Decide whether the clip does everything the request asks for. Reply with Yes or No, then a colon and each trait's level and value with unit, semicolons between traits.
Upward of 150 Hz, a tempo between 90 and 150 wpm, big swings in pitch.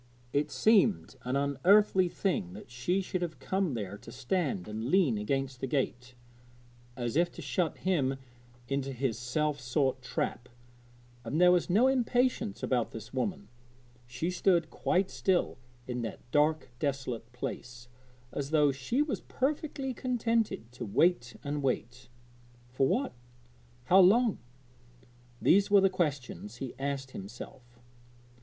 No: medium, 140 Hz; average, 140 wpm; wide, 7.1 semitones